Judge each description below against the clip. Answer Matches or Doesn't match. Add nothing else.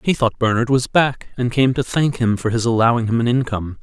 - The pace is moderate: Doesn't match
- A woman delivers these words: Doesn't match